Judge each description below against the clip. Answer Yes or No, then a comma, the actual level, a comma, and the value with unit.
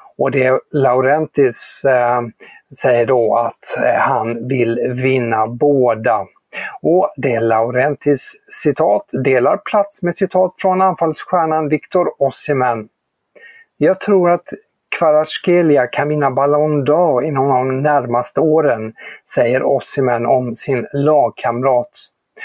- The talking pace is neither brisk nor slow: No, slow, 105 wpm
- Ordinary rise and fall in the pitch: Yes, average, 4.9 semitones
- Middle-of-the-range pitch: Yes, medium, 145 Hz